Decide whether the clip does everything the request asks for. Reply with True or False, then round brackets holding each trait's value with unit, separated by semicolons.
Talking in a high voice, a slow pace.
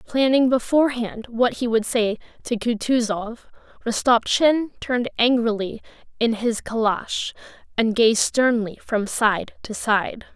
True (230 Hz; 120 wpm)